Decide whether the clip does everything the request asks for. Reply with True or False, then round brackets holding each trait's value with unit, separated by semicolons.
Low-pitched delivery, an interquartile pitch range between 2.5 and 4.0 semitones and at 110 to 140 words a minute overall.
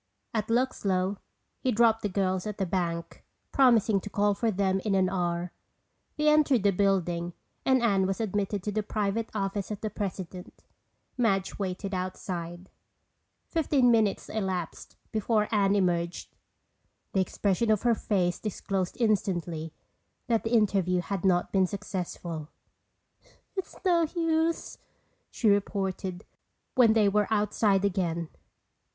False (200 Hz; 3.0 semitones; 135 wpm)